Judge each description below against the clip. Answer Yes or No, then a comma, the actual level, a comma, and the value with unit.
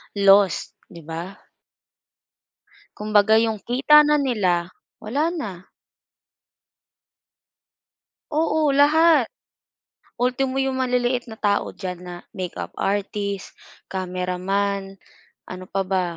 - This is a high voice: Yes, high, 205 Hz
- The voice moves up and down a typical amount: No, wide, 5.7 semitones